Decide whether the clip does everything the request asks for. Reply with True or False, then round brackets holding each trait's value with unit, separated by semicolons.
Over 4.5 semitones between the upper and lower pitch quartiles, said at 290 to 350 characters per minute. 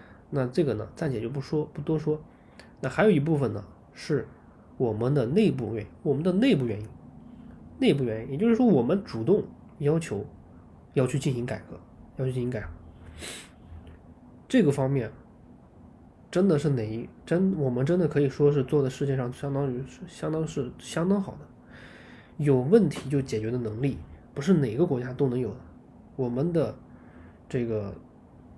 False (5.1 semitones; 250 characters per minute)